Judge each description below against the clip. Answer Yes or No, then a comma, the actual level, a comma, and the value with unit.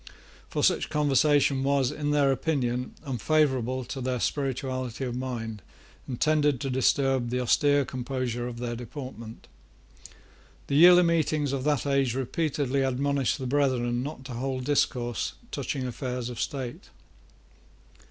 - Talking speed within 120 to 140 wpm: Yes, slow, 135 wpm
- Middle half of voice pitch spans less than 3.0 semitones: Yes, narrow, 2.5 semitones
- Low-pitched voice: Yes, low, 130 Hz